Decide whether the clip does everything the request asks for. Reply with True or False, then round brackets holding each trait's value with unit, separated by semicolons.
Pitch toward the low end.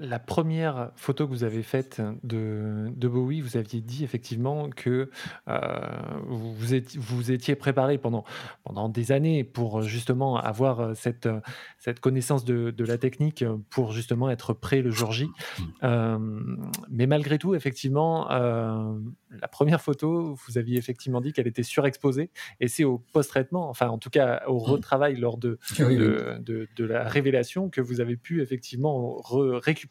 True (125 Hz)